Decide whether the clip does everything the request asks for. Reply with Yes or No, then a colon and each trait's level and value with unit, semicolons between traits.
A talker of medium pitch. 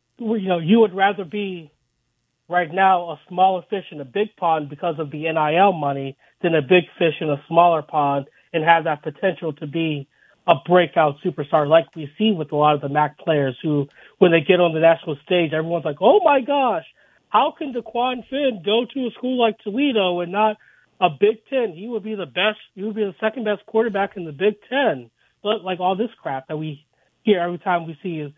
Yes: medium, 180 Hz